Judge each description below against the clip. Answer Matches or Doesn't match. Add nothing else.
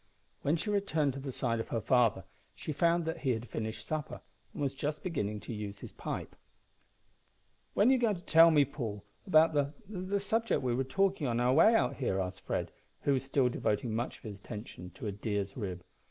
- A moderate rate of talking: Doesn't match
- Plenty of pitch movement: Matches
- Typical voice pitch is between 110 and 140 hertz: Matches